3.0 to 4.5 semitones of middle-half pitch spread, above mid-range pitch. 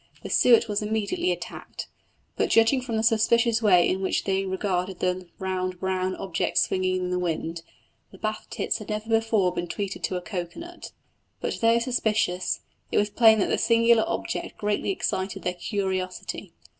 Yes: average, 3.4 semitones; high, 200 Hz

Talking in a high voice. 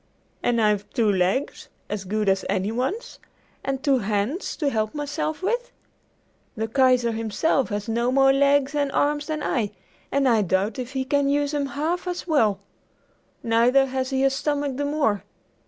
Yes: very high, 265 Hz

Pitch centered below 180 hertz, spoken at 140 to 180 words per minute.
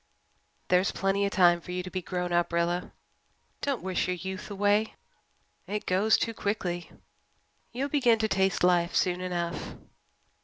No: medium, 185 Hz; average, 155 wpm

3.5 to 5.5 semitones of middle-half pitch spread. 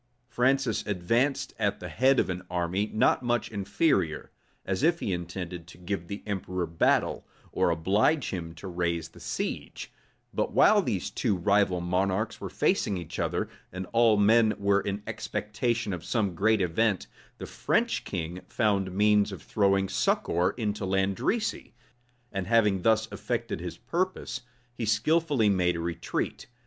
Yes: average, 3.8 semitones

